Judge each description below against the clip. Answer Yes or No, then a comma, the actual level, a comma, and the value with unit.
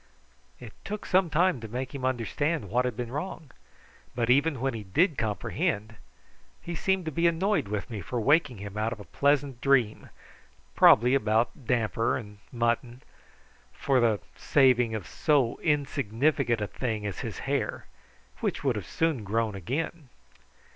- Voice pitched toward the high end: No, low, 125 Hz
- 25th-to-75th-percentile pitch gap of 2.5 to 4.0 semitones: No, average, 4.8 semitones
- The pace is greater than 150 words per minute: Yes, average, 160 wpm